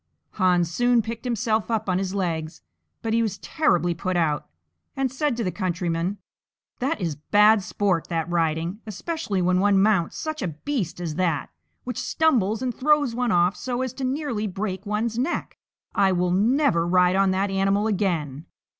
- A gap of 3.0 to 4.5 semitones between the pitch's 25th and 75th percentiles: No, average, 4.9 semitones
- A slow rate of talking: No, average, 175 wpm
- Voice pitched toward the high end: Yes, high, 195 Hz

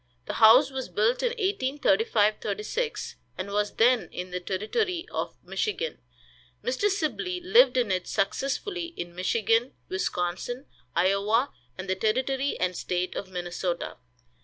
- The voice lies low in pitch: No, high, 225 Hz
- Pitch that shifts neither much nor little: No, wide, 7.5 semitones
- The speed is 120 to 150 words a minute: Yes, slow, 135 wpm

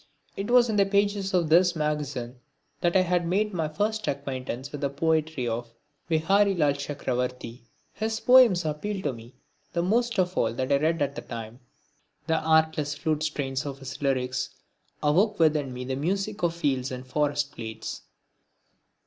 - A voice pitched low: No, medium, 150 Hz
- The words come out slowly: No, average, 165 wpm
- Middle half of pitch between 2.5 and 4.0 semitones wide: No, wide, 5.6 semitones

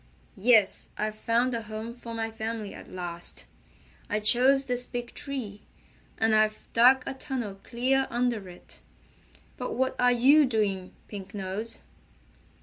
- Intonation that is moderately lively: Yes, average, 3.0 semitones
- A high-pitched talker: Yes, high, 230 Hz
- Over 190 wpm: No, average, 145 wpm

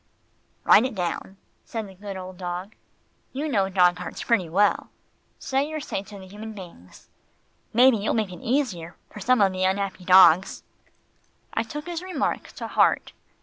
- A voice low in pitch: No, high, 200 Hz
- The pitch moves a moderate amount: Yes, average, 4.2 semitones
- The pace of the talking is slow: No, average, 170 wpm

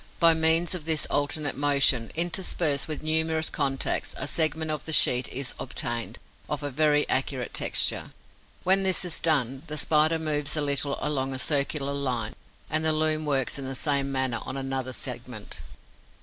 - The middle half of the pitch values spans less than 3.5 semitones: Yes, average, 2.8 semitones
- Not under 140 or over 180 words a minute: Yes, average, 170 wpm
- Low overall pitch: No, medium, 145 Hz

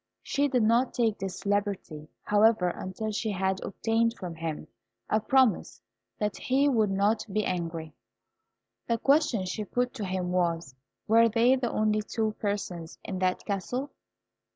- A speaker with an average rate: Yes, average, 155 wpm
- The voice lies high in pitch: Yes, high, 210 Hz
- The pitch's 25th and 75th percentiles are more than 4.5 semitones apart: No, average, 3.8 semitones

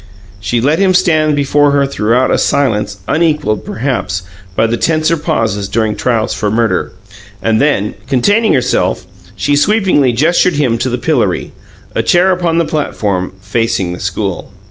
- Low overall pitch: Yes, low, 130 Hz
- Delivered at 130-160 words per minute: Yes, average, 155 wpm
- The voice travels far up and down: Yes, wide, 6.4 semitones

